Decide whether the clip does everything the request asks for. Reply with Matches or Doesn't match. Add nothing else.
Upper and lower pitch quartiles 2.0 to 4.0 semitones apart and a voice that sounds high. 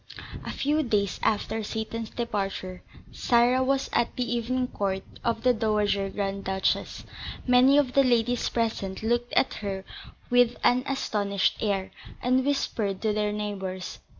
Matches